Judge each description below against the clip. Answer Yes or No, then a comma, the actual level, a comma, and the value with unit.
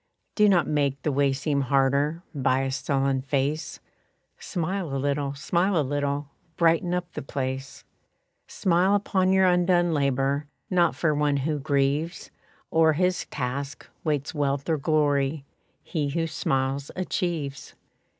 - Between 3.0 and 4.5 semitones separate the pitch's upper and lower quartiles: Yes, average, 3.6 semitones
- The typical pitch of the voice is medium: Yes, medium, 145 Hz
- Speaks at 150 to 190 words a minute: No, average, 140 wpm